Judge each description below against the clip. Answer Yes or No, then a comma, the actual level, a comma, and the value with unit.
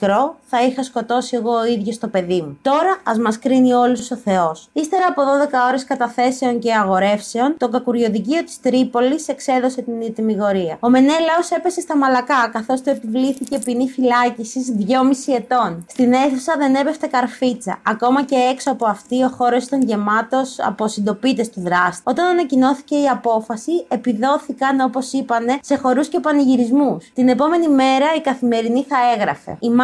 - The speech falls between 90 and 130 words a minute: No, average, 155 wpm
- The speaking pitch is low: No, very high, 255 Hz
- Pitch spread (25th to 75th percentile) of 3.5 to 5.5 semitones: No, average, 2.7 semitones